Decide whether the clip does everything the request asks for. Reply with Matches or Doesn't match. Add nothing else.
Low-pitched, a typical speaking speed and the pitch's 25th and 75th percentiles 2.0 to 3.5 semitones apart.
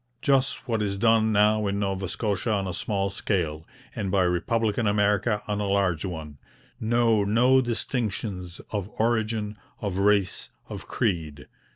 Matches